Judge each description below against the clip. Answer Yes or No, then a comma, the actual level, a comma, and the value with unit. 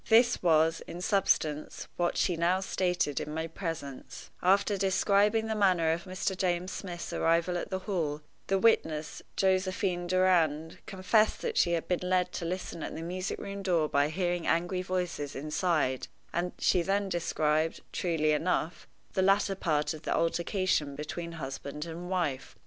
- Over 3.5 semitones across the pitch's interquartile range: No, average, 2.8 semitones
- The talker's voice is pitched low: No, medium, 175 Hz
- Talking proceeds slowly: No, average, 160 wpm